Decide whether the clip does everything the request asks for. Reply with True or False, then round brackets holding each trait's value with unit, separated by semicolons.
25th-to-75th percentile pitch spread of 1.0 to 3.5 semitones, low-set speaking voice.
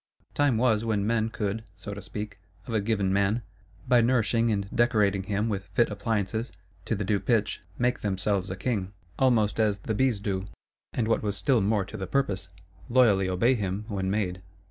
True (2.6 semitones; 105 Hz)